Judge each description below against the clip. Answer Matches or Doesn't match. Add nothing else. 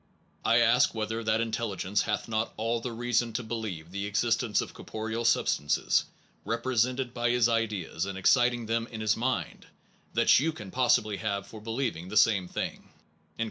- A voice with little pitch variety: Matches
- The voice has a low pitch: Matches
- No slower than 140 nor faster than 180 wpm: Matches